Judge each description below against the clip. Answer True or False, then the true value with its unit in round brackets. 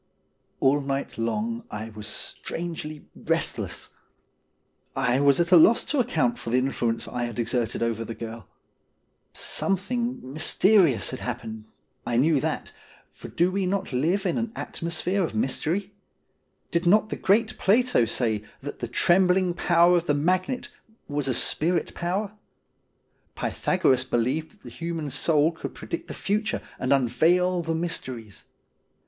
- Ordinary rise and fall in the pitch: False (6.7 semitones)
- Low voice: False (155 Hz)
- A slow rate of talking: False (150 wpm)